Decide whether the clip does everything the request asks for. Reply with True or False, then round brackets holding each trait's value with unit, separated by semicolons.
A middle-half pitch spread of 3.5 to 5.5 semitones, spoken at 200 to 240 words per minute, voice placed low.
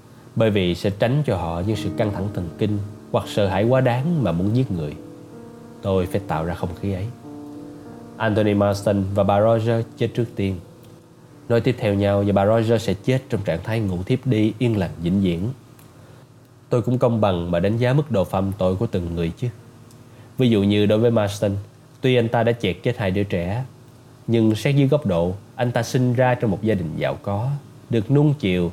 True (3.8 semitones; 215 wpm; 115 Hz)